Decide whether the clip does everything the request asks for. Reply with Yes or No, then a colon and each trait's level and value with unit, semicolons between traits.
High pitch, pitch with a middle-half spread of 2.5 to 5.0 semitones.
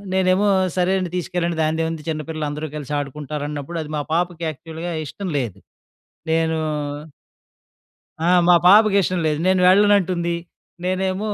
No: medium, 170 Hz; average, 3.2 semitones